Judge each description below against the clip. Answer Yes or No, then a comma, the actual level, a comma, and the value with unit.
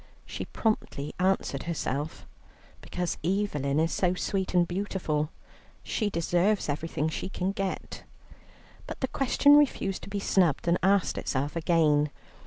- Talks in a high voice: No, medium, 175 Hz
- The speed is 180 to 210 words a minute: No, slow, 135 wpm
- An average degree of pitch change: Yes, average, 4.2 semitones